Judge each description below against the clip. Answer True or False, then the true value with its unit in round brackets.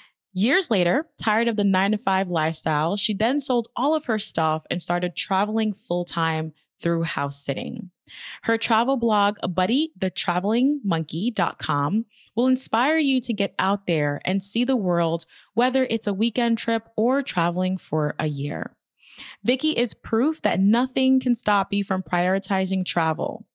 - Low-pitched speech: False (200 Hz)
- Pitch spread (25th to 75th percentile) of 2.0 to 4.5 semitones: False (5.0 semitones)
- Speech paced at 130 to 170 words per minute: True (150 wpm)